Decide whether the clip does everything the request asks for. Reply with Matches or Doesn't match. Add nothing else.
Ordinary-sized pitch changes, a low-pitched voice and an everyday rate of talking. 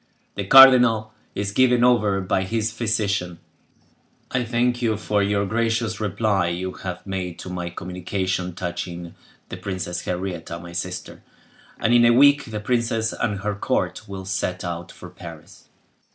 Matches